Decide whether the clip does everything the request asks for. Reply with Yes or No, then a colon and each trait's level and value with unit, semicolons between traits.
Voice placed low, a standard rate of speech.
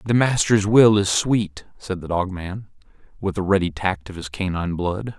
Yes: very low, 95 Hz; average, 195 wpm